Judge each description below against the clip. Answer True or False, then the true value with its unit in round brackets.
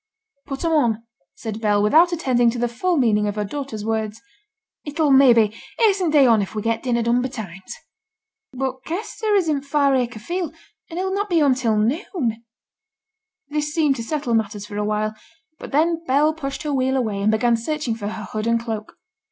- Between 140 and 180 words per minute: False (200 wpm)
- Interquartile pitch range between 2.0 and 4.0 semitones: False (5.5 semitones)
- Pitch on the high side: True (250 Hz)